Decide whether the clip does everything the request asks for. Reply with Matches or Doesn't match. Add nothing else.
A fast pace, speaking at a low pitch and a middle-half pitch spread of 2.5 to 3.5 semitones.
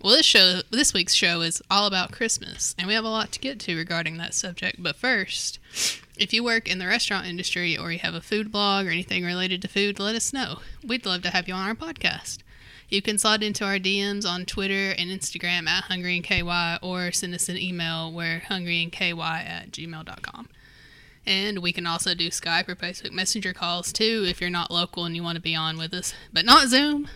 Doesn't match